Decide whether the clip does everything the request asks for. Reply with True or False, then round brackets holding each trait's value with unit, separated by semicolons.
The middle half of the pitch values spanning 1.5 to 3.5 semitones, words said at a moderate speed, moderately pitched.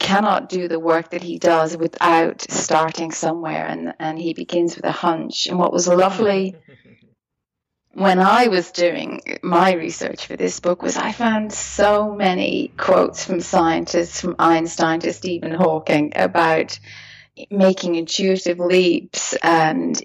True (2.4 semitones; 145 wpm; 175 Hz)